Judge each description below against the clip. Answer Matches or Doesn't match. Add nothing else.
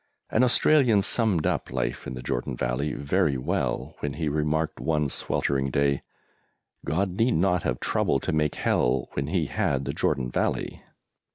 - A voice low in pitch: Matches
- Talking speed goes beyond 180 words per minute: Doesn't match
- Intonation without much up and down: Doesn't match